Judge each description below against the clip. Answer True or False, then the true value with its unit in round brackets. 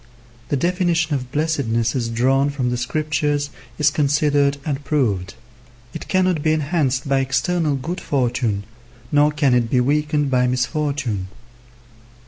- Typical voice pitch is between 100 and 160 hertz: True (140 Hz)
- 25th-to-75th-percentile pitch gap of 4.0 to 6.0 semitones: False (3.2 semitones)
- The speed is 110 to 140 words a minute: True (135 wpm)